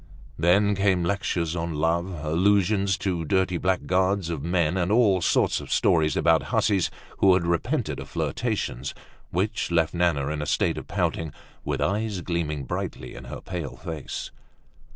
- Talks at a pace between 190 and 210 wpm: No, average, 155 wpm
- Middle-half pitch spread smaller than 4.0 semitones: Yes, average, 2.9 semitones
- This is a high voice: No, very low, 90 Hz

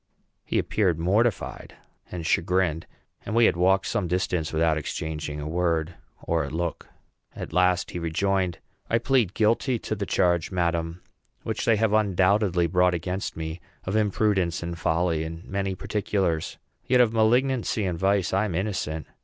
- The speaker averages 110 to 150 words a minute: No, average, 160 wpm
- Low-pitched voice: Yes, very low, 90 Hz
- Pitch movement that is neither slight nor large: Yes, average, 3.8 semitones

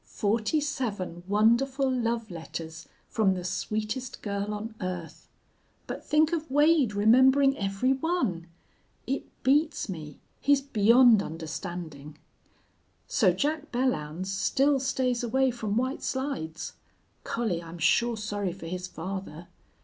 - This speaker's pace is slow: Yes, slow, 120 wpm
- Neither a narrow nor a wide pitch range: No, wide, 6.4 semitones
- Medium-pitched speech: No, high, 215 Hz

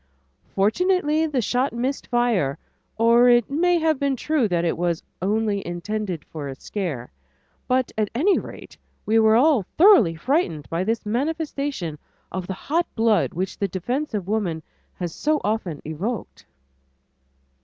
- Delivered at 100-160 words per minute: Yes, average, 150 wpm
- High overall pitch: Yes, high, 220 Hz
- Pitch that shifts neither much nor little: No, wide, 7.5 semitones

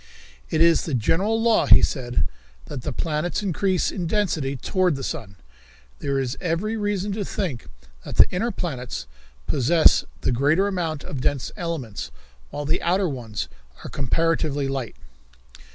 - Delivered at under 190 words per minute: Yes, average, 150 wpm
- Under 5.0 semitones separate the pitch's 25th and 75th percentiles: No, wide, 5.5 semitones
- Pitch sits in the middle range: Yes, medium, 160 Hz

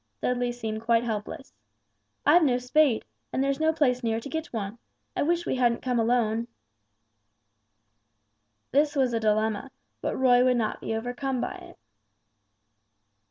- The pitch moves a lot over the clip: No, average, 3.1 semitones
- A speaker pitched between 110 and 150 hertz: No, high, 245 Hz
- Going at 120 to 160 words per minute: Yes, average, 150 wpm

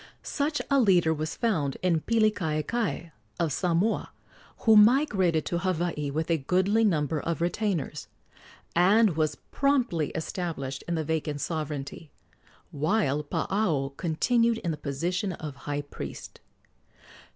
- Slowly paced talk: Yes, slow, 125 wpm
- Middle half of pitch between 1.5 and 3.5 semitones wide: No, wide, 5.4 semitones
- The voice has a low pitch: No, medium, 170 Hz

